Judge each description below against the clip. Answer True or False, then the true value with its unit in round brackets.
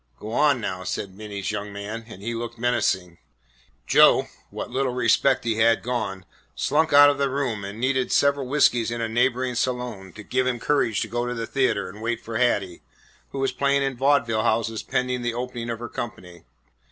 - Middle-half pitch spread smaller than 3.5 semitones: True (2.9 semitones)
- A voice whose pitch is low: True (120 Hz)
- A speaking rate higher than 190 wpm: True (200 wpm)